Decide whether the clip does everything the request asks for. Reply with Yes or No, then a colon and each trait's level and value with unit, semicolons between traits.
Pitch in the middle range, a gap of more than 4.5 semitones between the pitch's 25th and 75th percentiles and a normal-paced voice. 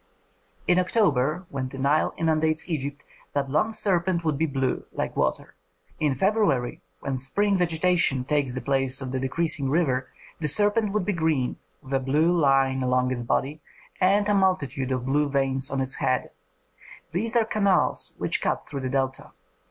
Yes: medium, 145 Hz; average, 5.0 semitones; average, 170 wpm